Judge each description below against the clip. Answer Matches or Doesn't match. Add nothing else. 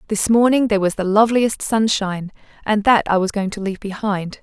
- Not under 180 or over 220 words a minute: Matches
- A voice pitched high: Matches